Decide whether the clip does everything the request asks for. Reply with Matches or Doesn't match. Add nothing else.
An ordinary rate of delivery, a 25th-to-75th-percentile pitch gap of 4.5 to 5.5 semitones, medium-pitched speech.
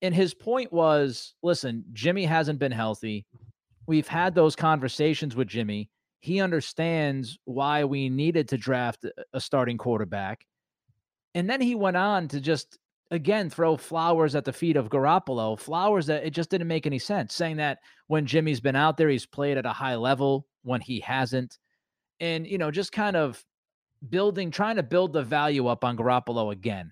Matches